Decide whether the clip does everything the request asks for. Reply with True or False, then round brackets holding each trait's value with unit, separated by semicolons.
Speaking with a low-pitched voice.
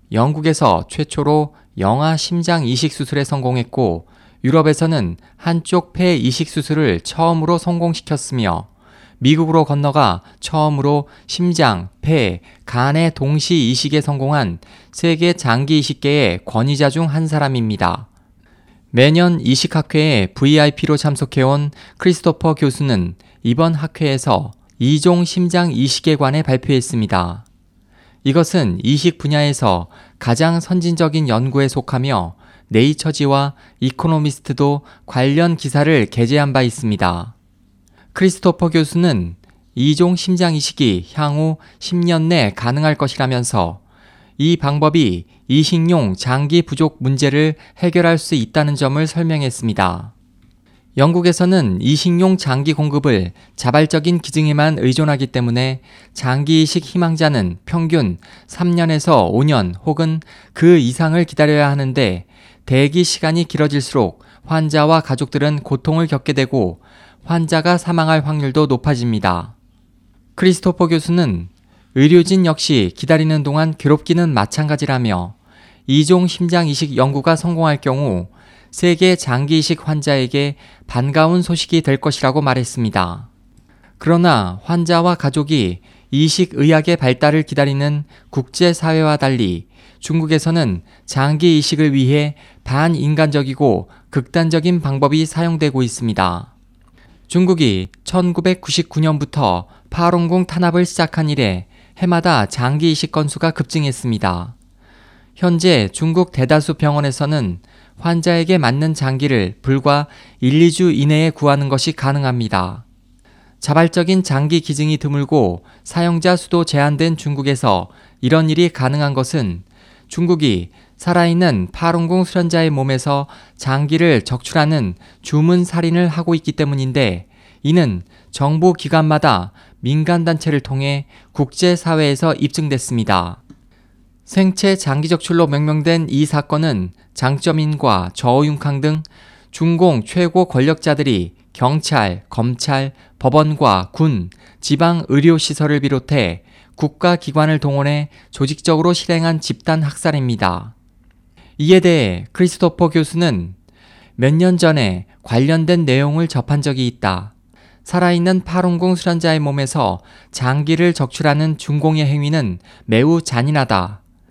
False (145 Hz)